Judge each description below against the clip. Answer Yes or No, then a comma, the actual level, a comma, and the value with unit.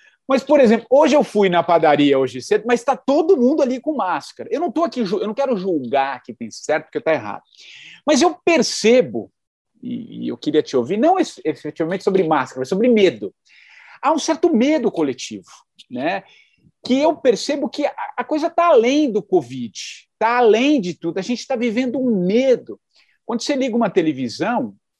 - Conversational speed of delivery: Yes, average, 185 wpm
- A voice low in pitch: No, high, 240 Hz